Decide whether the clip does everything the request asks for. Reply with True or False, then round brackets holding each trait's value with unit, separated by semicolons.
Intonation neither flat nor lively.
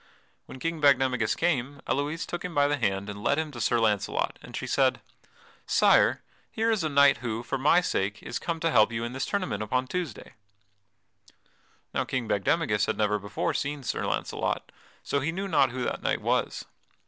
False (5.9 semitones)